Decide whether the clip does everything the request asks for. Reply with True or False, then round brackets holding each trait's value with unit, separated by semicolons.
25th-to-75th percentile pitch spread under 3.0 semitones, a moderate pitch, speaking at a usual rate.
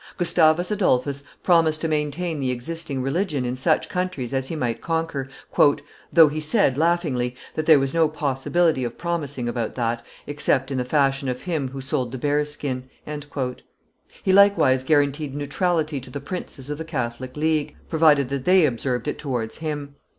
False (3.7 semitones; 145 Hz; 170 wpm)